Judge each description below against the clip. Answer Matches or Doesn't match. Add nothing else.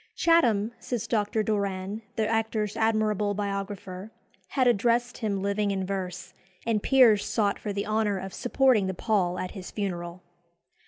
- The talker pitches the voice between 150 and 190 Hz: Doesn't match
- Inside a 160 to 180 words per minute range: Doesn't match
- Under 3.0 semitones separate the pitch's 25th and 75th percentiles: Matches